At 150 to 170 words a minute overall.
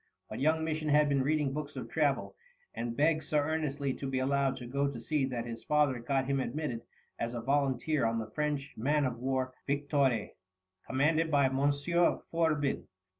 No: average, 180 wpm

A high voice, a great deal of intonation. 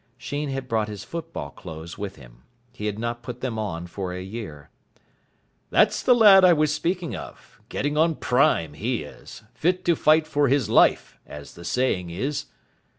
No: low, 120 Hz; wide, 8.6 semitones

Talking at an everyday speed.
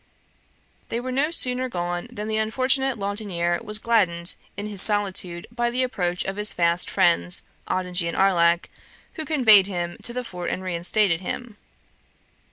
Yes: average, 160 wpm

